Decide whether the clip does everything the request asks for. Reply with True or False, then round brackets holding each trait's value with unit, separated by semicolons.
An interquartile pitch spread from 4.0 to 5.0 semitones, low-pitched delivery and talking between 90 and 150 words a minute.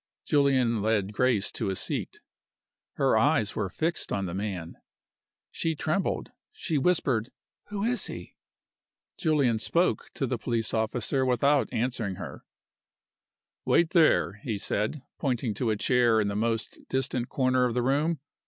True (4.7 semitones; 125 Hz; 145 wpm)